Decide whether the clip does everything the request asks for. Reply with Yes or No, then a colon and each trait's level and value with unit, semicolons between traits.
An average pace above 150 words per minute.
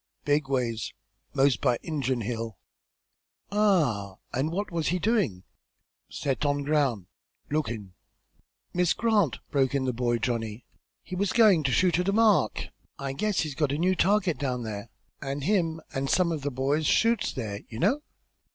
Yes: average, 165 wpm